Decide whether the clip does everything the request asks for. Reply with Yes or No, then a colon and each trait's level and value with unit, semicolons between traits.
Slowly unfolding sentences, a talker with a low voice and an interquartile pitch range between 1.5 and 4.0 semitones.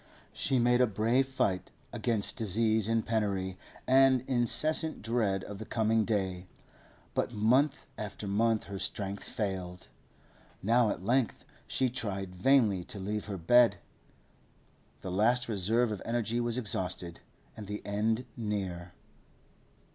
Yes: slow, 130 wpm; low, 110 Hz; average, 3.5 semitones